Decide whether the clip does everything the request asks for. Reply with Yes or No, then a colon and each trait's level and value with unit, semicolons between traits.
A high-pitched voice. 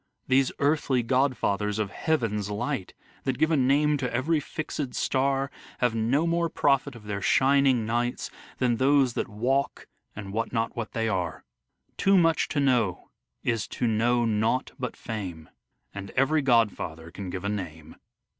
No: low, 120 Hz